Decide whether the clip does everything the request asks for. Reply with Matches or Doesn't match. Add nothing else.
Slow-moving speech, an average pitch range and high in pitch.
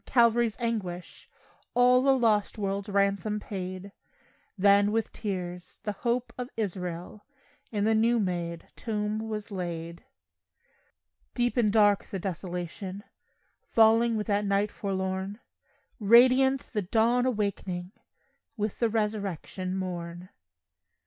Matches